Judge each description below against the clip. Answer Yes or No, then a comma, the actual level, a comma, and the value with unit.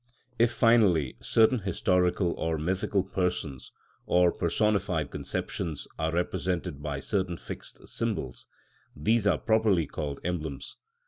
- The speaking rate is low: Yes, slow, 115 wpm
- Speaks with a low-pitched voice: Yes, very low, 90 Hz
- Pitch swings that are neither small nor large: Yes, average, 4.6 semitones